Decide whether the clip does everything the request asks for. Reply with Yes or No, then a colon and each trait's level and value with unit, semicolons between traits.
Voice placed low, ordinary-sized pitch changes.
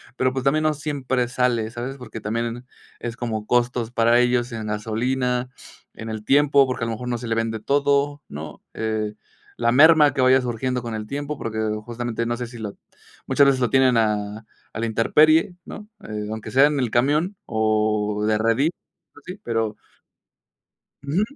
Yes: low, 120 Hz; average, 3.5 semitones